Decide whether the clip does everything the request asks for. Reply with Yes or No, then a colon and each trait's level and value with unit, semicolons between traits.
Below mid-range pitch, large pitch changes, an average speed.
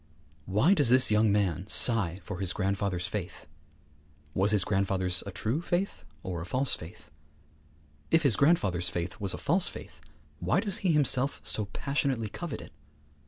Yes: low, 105 Hz; wide, 6.9 semitones; average, 165 wpm